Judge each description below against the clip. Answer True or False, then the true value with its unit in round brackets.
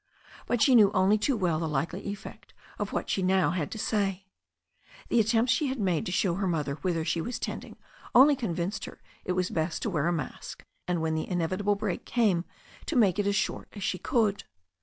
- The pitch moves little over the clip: False (4.0 semitones)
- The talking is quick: True (215 wpm)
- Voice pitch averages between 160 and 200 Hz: True (190 Hz)